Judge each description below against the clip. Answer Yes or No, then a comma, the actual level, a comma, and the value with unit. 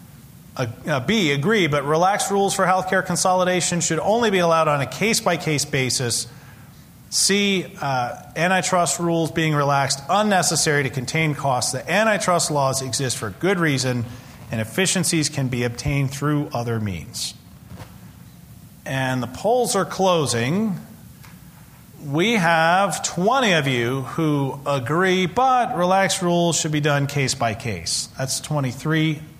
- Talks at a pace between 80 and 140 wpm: Yes, slow, 135 wpm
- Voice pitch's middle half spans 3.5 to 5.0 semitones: No, wide, 5.5 semitones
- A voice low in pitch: No, medium, 155 Hz